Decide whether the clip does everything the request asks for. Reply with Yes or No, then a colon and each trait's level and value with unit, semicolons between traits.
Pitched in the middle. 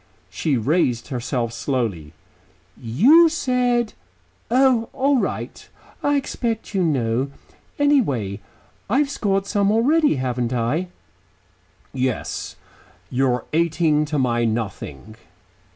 Yes: medium, 150 Hz